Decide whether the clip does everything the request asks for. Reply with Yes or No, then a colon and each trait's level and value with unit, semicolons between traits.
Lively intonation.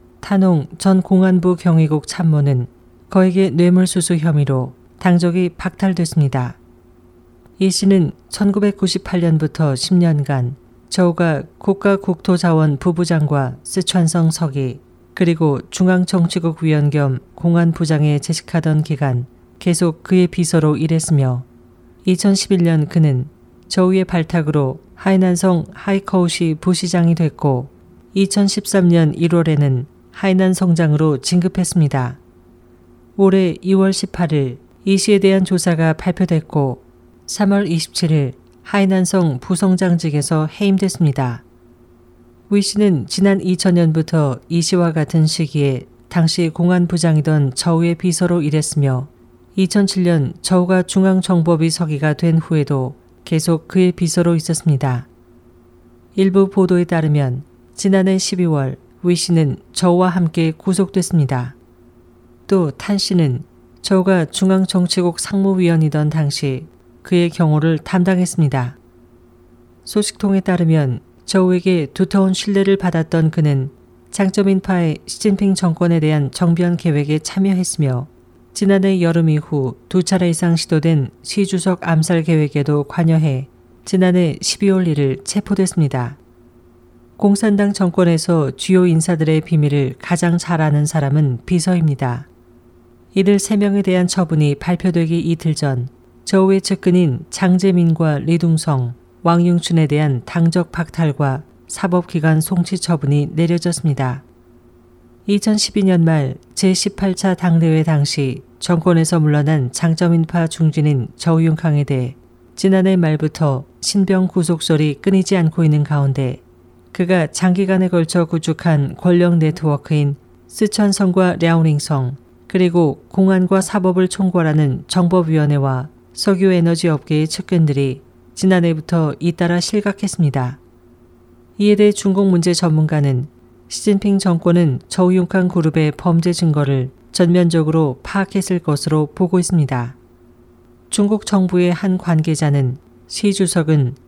No: average, 4.8 semitones